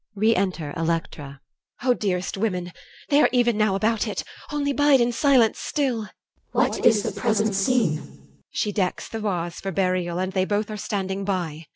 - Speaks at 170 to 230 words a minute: Yes, average, 190 wpm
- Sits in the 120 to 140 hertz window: No, high, 205 Hz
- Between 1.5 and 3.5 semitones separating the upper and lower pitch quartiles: No, average, 3.9 semitones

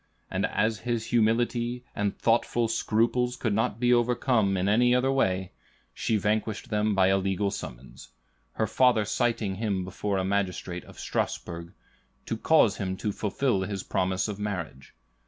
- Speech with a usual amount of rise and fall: Yes, average, 3.6 semitones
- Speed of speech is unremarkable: Yes, average, 155 wpm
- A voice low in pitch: Yes, low, 105 Hz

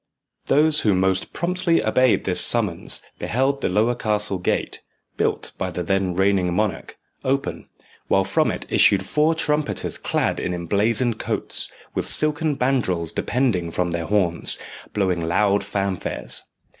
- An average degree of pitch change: No, wide, 6.2 semitones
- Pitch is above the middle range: No, low, 105 Hz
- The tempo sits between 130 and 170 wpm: Yes, average, 140 wpm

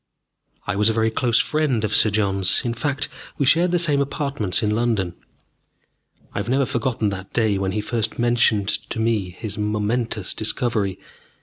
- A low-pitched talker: Yes, low, 110 Hz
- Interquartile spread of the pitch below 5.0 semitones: Yes, average, 3.2 semitones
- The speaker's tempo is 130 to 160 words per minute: No, average, 175 wpm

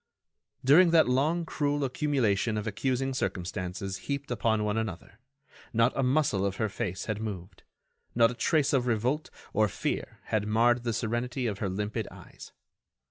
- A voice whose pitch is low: Yes, low, 115 Hz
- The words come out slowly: No, average, 160 wpm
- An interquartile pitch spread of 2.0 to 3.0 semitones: No, average, 4.4 semitones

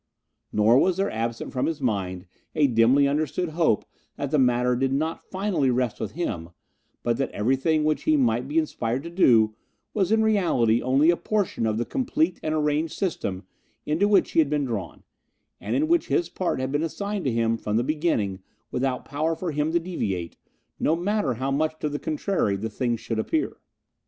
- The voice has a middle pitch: Yes, medium, 145 Hz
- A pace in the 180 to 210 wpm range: Yes, average, 195 wpm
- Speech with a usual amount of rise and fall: No, wide, 6.0 semitones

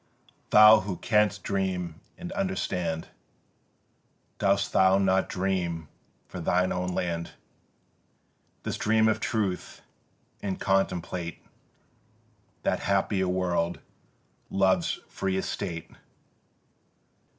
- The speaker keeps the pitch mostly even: Yes, narrow, 2.0 semitones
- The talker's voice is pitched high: No, very low, 95 Hz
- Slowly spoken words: Yes, slow, 90 wpm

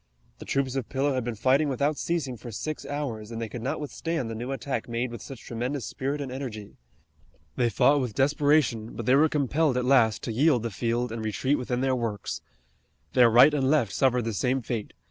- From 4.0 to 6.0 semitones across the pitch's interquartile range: No, average, 3.3 semitones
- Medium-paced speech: No, fast, 215 wpm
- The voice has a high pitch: No, low, 125 Hz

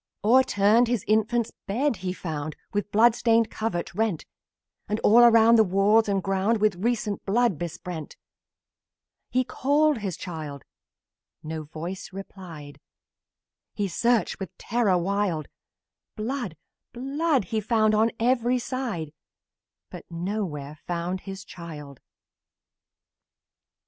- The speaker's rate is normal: No, slow, 115 wpm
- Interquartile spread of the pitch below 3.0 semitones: No, average, 5.0 semitones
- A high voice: Yes, high, 205 Hz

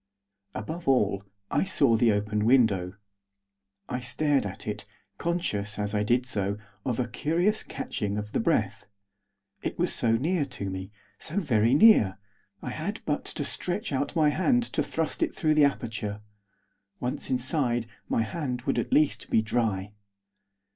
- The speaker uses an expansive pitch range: Yes, wide, 6.2 semitones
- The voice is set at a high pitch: No, low, 120 Hz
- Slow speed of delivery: No, average, 160 wpm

